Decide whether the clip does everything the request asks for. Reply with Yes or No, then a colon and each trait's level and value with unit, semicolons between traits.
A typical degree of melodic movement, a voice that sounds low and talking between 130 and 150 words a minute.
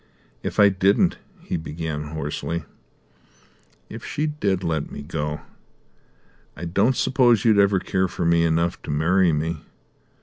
Yes: average, 3.8 semitones; very low, 85 Hz; average, 140 wpm